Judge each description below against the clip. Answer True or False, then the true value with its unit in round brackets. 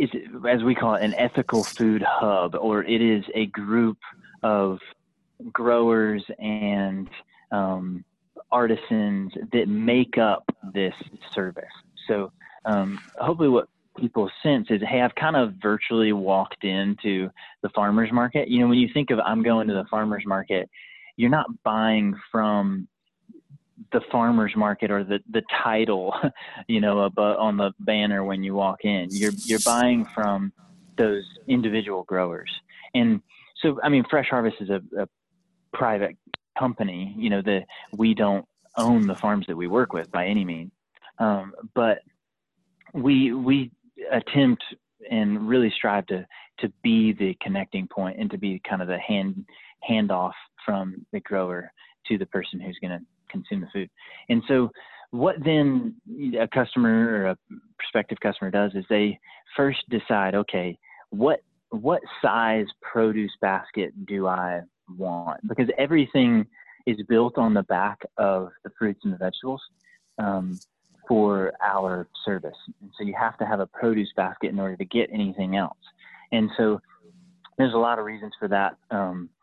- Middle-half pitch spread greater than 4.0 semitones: True (4.8 semitones)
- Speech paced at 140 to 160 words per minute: True (155 wpm)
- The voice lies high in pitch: False (110 Hz)